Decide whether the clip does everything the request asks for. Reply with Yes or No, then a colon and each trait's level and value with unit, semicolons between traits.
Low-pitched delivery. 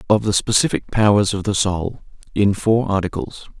Yes: low, 100 Hz